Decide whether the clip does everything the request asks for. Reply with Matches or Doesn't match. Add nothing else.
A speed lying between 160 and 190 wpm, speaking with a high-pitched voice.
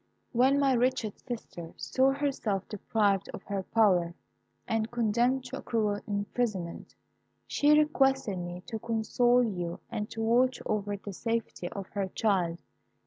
Doesn't match